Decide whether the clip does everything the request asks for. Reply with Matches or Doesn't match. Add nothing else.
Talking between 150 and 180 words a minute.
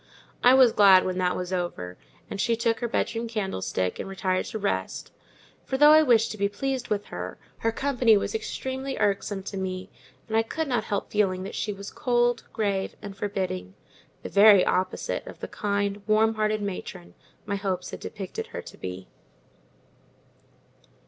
Matches